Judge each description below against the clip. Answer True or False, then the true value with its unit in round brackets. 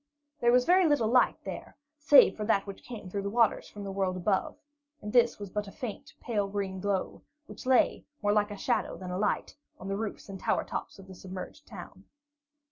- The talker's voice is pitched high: True (205 Hz)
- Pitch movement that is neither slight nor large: True (3.5 semitones)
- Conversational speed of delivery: False (215 wpm)